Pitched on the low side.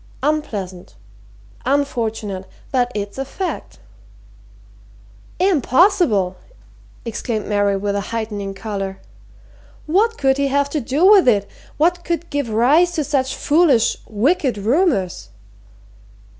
No: very high, 255 Hz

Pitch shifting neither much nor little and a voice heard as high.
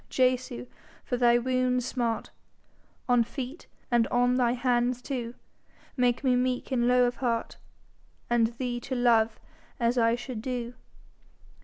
No: narrow, 1.1 semitones; high, 245 Hz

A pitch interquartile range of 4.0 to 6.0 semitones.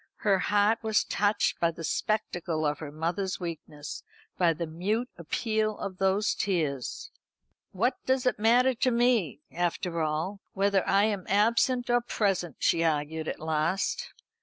Yes: average, 4.8 semitones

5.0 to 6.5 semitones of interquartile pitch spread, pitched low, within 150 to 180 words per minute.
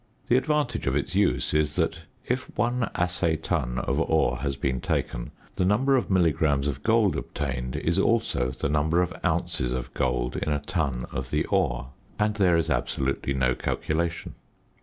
Yes: wide, 5.4 semitones; very low, 75 Hz; average, 175 wpm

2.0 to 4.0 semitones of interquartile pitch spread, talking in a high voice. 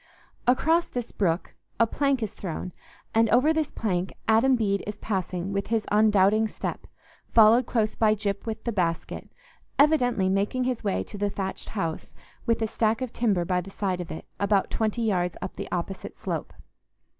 Yes: average, 3.2 semitones; high, 215 Hz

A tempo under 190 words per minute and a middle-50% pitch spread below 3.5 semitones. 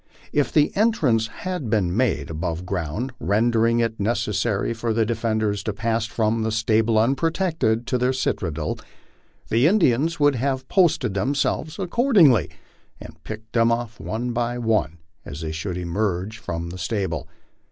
No: average, 155 wpm; average, 4.4 semitones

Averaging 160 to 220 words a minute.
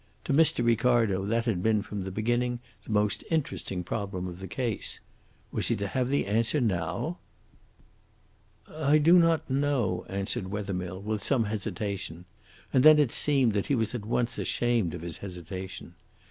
Yes: average, 165 wpm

